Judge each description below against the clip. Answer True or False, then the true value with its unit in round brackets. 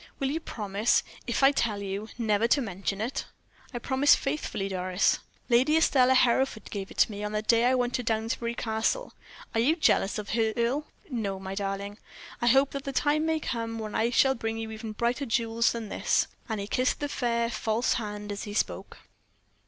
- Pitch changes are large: False (3.6 semitones)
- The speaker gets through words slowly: False (200 wpm)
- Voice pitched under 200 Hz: False (230 Hz)